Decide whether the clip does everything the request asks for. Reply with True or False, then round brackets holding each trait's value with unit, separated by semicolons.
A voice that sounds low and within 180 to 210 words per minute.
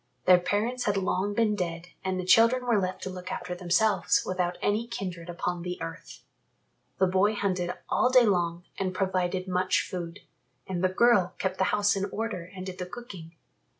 False (185 Hz; 185 wpm)